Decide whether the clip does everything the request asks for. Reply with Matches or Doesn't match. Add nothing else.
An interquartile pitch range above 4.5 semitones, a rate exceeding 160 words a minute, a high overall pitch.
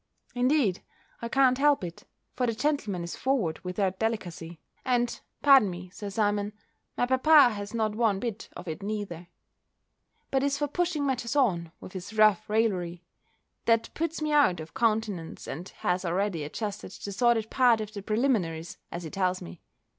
Matches